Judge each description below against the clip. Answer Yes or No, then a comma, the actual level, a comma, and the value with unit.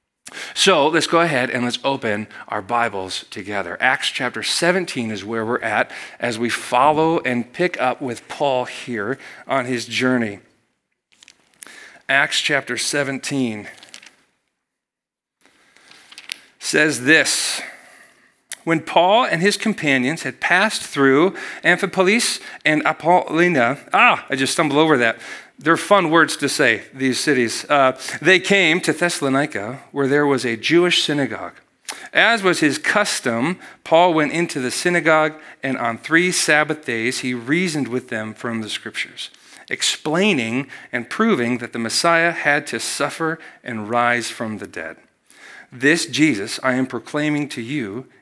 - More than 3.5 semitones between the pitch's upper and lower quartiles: Yes, average, 5.1 semitones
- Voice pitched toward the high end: No, low, 135 Hz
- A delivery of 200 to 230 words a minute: No, average, 140 wpm